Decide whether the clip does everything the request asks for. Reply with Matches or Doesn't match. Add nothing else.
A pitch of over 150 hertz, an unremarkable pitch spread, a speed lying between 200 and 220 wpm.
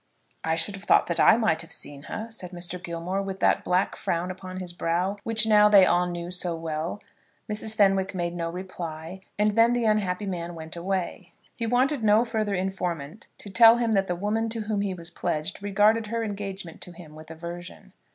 Matches